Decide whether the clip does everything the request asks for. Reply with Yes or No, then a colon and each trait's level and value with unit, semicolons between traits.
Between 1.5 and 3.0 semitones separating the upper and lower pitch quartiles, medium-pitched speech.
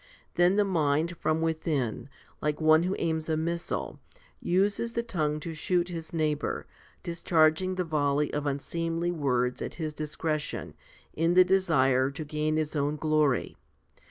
Yes: narrow, 2.4 semitones; medium, 155 Hz